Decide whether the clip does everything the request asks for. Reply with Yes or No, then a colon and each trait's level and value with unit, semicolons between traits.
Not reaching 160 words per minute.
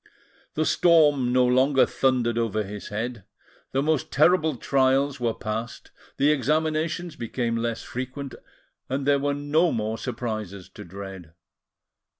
Yes: slow, 135 wpm